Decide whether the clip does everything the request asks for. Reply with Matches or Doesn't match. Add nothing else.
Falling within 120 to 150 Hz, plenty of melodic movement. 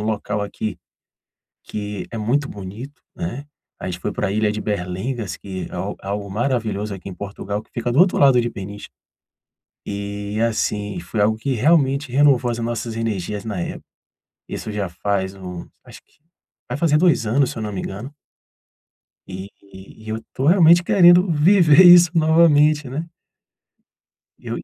Doesn't match